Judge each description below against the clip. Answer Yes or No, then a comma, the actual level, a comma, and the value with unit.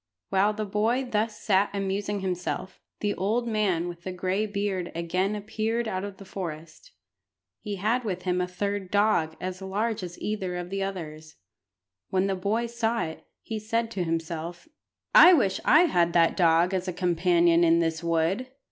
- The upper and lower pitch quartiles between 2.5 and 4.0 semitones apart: Yes, average, 3.3 semitones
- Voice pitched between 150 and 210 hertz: Yes, high, 190 Hz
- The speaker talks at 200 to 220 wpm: No, average, 175 wpm